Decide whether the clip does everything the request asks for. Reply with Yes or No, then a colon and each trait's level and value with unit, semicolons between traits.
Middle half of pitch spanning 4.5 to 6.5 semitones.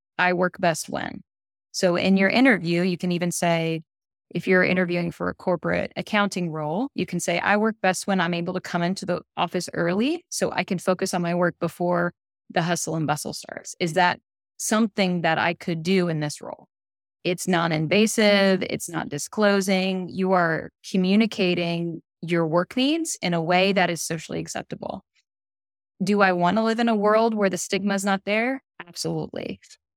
No: narrow, 2.4 semitones